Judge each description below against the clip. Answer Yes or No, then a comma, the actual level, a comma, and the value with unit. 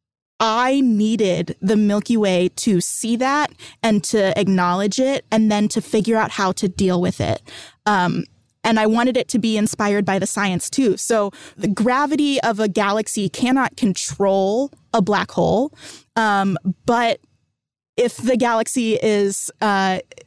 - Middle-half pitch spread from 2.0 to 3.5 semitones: Yes, average, 3.2 semitones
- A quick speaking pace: No, average, 155 wpm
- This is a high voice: Yes, high, 215 Hz